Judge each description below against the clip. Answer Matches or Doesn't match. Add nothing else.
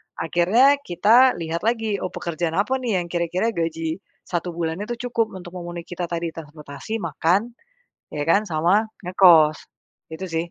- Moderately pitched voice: Matches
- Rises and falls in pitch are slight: Doesn't match